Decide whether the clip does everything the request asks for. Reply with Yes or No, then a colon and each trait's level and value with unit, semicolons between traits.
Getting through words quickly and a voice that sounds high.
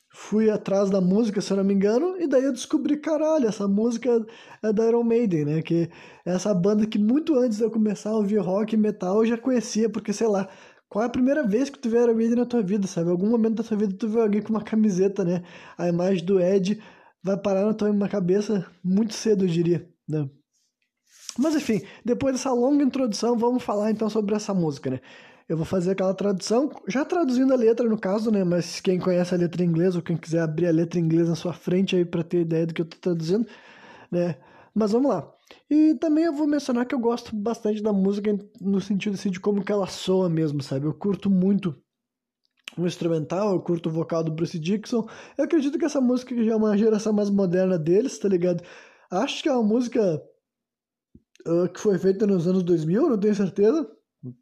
Yes: fast, 220 wpm; high, 205 Hz